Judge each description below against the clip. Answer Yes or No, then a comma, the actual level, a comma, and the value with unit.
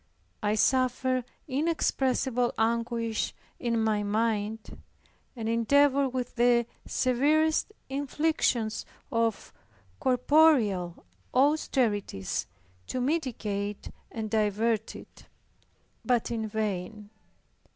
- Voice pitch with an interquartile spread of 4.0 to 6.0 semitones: No, average, 3.3 semitones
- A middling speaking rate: No, slow, 80 wpm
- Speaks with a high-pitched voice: Yes, high, 235 Hz